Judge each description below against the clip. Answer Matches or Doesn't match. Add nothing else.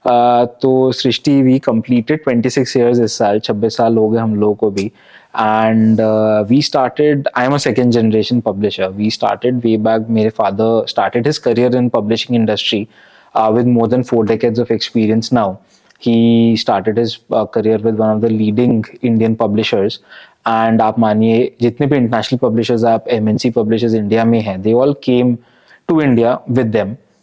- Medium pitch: Doesn't match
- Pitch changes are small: Matches